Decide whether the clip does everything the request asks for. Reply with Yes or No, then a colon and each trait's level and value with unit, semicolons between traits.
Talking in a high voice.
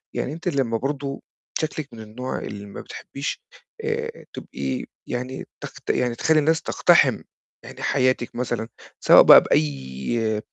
No: low, 130 Hz